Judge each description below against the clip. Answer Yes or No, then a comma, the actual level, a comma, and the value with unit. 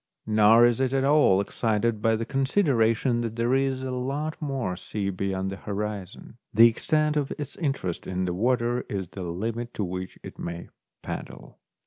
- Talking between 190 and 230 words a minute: No, average, 180 wpm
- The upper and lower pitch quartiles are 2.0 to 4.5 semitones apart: No, average, 5.2 semitones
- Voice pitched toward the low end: Yes, low, 115 Hz